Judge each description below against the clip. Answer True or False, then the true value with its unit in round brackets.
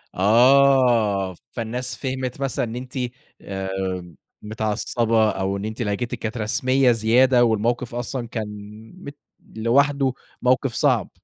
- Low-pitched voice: True (115 Hz)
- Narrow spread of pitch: False (3.1 semitones)